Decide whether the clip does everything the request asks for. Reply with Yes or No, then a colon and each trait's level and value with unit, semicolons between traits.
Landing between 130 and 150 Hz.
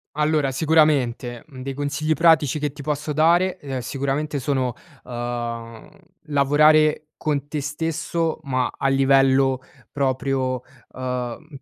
Yes: medium, 140 Hz